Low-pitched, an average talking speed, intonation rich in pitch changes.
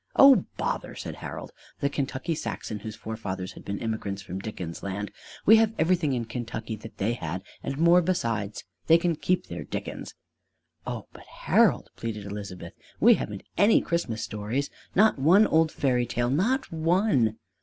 Yes: low, 120 Hz; average, 165 wpm; wide, 8.2 semitones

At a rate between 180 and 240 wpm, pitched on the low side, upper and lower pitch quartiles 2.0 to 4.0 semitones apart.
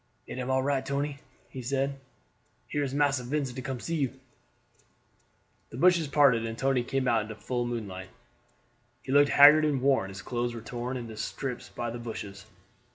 Yes: average, 185 wpm; low, 130 Hz; average, 2.9 semitones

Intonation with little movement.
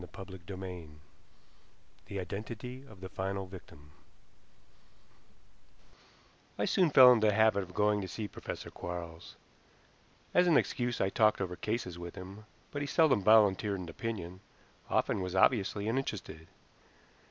No: average, 3.3 semitones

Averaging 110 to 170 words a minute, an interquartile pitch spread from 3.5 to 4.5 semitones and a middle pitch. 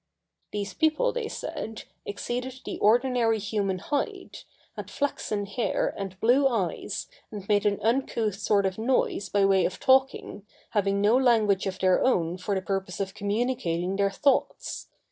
No: average, 155 wpm; average, 4.2 semitones; high, 205 Hz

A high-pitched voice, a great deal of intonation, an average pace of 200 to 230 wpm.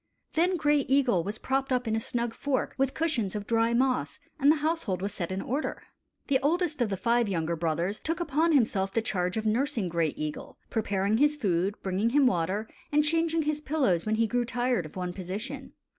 Yes: high, 230 Hz; wide, 6.9 semitones; fast, 205 wpm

